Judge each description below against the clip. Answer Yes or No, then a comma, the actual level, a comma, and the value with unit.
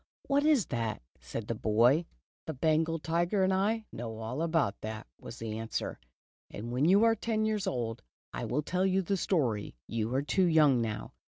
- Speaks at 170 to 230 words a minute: Yes, average, 190 wpm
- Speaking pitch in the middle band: Yes, medium, 155 Hz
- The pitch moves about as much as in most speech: No, wide, 8.7 semitones